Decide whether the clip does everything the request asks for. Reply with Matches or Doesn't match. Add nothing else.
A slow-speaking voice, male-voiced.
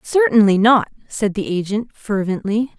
Doesn't match